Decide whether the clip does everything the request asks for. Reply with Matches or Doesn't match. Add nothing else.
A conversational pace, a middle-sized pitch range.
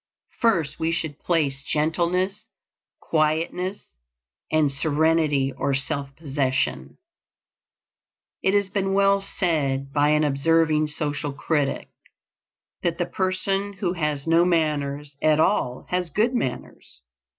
Doesn't match